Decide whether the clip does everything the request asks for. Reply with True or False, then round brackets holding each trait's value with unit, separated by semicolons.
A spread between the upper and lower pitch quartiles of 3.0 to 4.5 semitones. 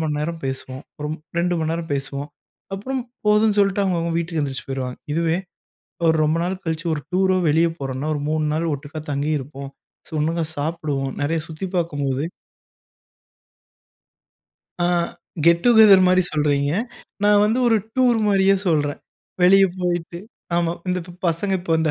True (3.9 semitones)